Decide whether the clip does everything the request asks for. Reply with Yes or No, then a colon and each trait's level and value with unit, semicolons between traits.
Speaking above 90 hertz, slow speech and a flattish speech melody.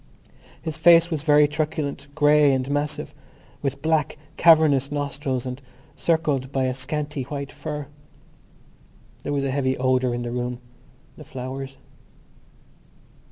Yes: medium, 140 Hz; slow, 125 wpm; narrow, 2.3 semitones